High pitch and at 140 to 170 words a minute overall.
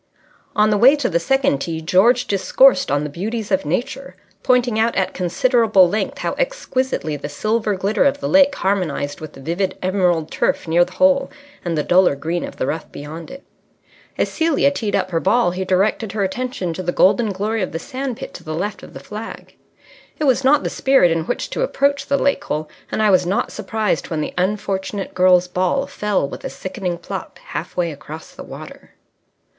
No: high, 195 Hz; fast, 205 wpm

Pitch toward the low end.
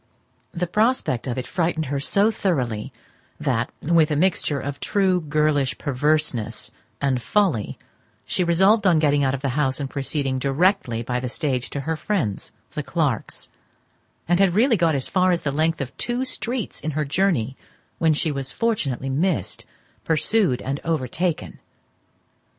No: medium, 150 Hz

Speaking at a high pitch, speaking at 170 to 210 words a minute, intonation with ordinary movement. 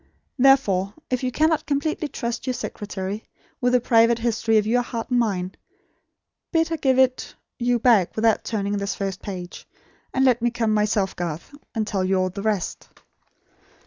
Yes: high, 225 Hz; average, 175 wpm; average, 4.0 semitones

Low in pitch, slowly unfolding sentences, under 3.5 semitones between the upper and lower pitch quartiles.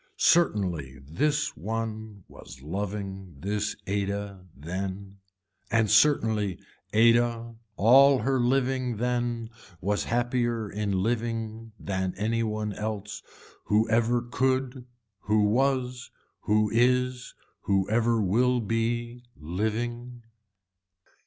Yes: low, 110 Hz; slow, 100 wpm; average, 3.0 semitones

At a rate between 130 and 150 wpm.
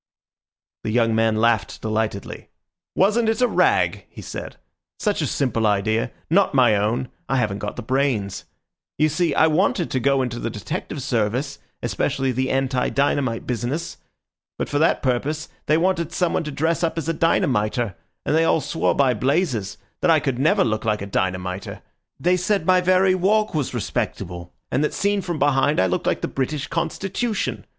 No: average, 175 wpm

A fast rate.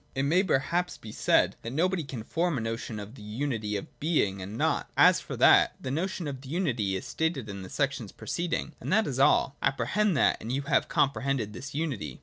Yes: fast, 225 wpm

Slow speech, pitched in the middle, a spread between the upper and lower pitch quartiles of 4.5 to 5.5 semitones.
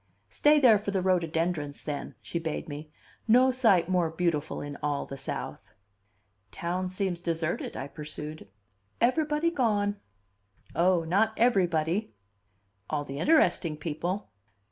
Yes: slow, 125 wpm; medium, 175 Hz; average, 5.1 semitones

